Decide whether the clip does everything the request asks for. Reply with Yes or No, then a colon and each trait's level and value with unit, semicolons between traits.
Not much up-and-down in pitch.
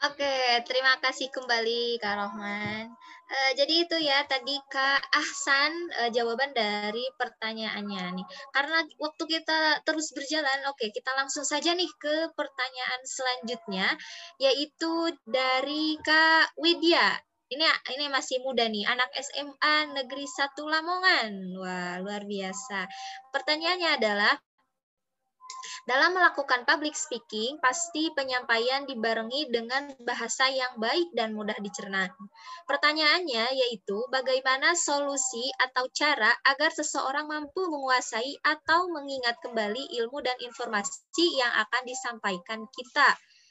No: average, 4.2 semitones